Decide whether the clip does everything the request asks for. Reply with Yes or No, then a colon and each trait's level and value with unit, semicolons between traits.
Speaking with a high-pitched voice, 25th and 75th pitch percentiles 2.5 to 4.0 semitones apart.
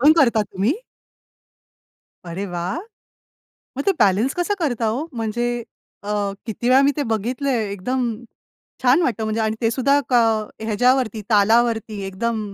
Yes: high, 235 Hz; average, 3.3 semitones